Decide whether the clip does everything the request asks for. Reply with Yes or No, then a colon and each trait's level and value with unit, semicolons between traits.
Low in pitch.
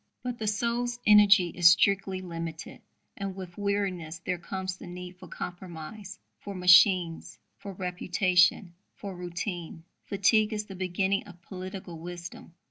No: medium, 185 Hz